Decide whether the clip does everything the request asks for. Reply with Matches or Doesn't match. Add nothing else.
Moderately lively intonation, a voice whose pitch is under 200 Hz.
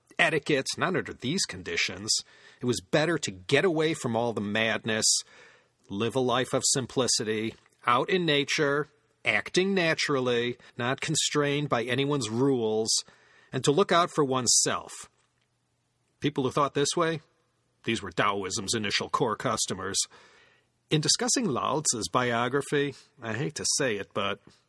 Matches